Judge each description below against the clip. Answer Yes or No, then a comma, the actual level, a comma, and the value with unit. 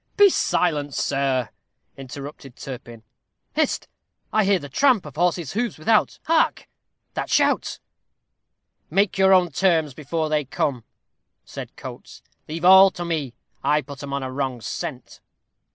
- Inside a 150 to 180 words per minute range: No, average, 140 wpm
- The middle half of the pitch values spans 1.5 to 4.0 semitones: No, wide, 5.5 semitones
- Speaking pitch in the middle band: Yes, medium, 150 Hz